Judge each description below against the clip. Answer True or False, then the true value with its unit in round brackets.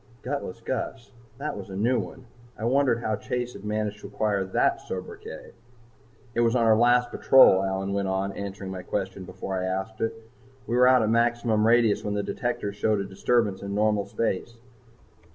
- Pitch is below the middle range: True (110 Hz)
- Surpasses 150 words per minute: True (190 wpm)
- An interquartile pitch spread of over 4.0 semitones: False (3.3 semitones)